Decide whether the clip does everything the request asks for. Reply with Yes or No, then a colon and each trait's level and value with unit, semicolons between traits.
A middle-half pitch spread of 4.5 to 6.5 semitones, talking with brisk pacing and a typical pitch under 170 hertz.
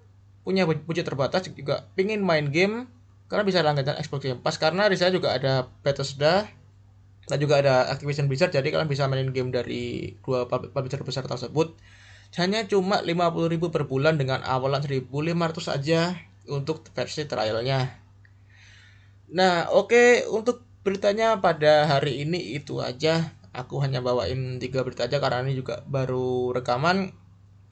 Yes: average, 5.1 semitones; fast, 145 wpm; medium, 140 Hz